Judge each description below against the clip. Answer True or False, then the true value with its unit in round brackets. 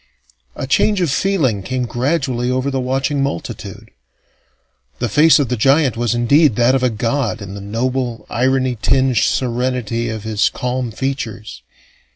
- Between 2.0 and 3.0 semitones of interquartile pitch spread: True (2.5 semitones)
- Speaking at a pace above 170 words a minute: False (155 wpm)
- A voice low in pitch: True (125 Hz)